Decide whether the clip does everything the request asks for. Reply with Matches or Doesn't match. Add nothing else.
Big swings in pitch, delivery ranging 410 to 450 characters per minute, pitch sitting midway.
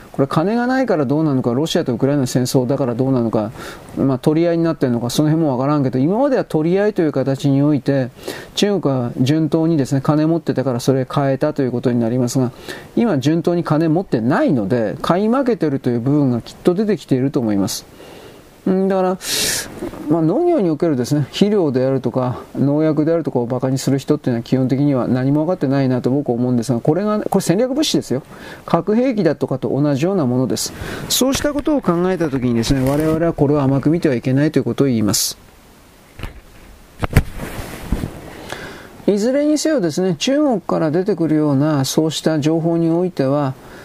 Doesn't match